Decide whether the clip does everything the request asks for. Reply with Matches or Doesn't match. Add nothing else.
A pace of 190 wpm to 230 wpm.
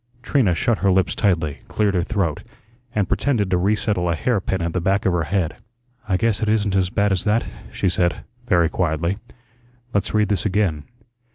Matches